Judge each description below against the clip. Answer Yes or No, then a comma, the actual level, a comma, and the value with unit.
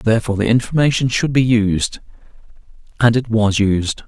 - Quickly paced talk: No, slow, 135 wpm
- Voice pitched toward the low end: Yes, low, 115 Hz